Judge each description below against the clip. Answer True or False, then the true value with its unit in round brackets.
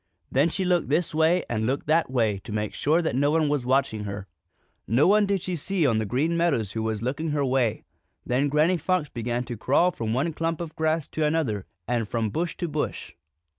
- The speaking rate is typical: False (220 wpm)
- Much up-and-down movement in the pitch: True (5.8 semitones)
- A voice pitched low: False (145 Hz)